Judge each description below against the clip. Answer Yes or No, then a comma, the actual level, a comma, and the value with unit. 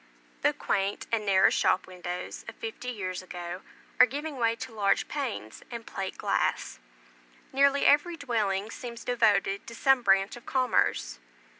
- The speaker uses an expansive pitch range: No, average, 4.5 semitones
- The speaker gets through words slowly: No, average, 150 wpm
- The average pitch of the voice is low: No, high, 225 Hz